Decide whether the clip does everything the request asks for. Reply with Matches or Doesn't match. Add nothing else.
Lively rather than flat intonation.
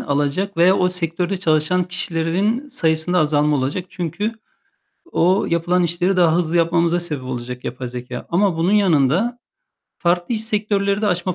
Doesn't match